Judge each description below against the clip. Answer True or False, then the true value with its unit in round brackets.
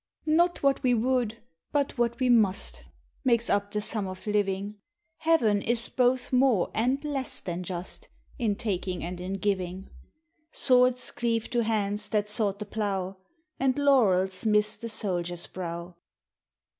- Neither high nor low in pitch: False (210 Hz)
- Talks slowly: False (145 wpm)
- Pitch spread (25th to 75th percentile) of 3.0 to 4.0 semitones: False (4.4 semitones)